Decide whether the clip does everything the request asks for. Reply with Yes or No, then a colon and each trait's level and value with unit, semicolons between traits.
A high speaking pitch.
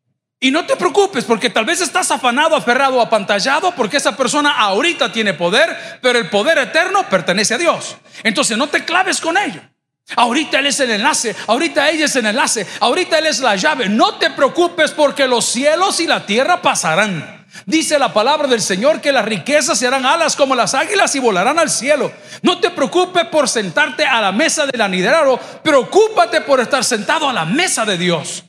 Yes: very high, 280 Hz